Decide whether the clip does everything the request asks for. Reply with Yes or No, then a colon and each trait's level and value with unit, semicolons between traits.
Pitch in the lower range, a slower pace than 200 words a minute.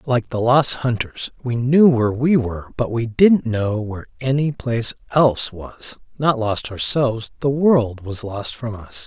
Yes: low, 120 Hz; average, 180 wpm